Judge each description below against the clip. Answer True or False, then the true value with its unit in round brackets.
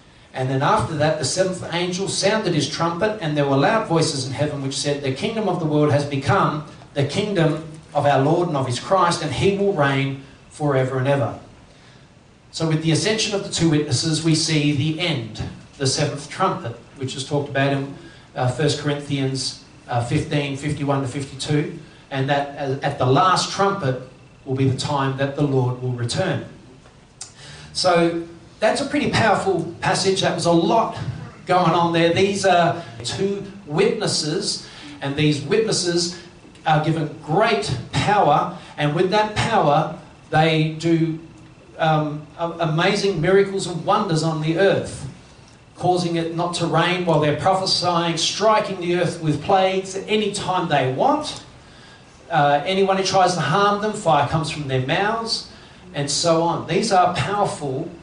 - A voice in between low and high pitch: True (160 Hz)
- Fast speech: False (160 wpm)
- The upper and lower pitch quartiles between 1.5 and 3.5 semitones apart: False (4.2 semitones)